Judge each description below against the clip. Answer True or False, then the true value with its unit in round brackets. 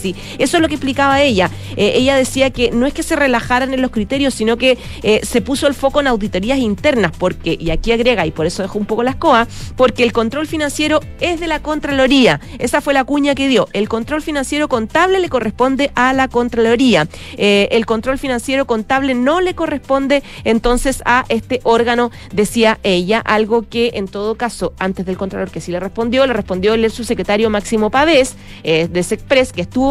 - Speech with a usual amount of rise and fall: True (4.0 semitones)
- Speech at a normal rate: False (205 wpm)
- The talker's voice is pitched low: False (245 Hz)